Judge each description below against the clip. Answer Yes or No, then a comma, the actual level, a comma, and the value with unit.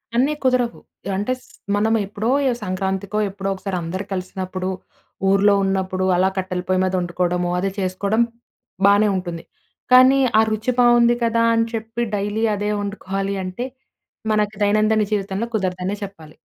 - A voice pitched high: Yes, high, 200 Hz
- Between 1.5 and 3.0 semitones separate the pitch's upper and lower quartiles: Yes, average, 2.7 semitones